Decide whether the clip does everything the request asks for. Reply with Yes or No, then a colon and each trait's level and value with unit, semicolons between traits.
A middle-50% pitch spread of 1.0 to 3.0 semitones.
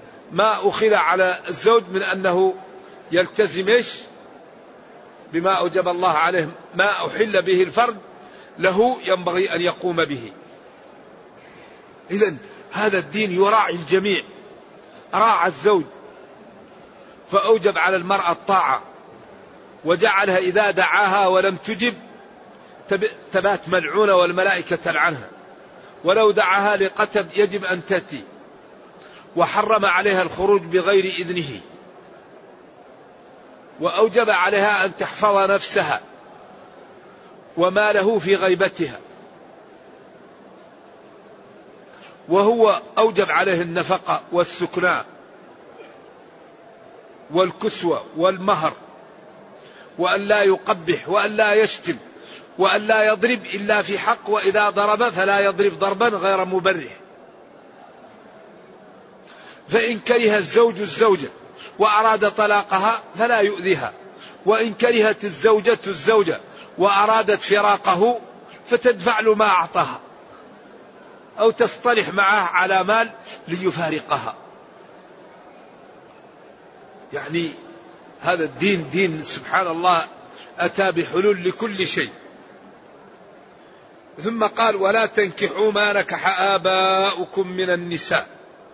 Yes: average, 2.7 semitones